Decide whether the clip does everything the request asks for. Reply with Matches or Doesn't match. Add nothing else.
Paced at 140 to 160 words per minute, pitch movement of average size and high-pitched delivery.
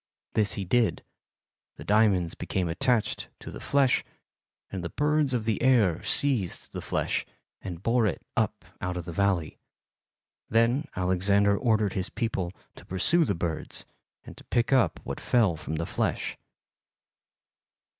Doesn't match